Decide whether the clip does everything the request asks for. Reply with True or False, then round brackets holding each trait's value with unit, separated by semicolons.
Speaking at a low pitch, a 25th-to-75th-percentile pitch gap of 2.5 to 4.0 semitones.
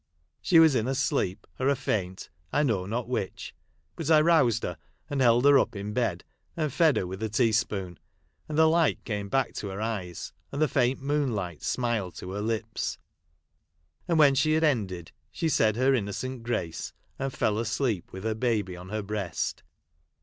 False (115 Hz; 5.3 semitones)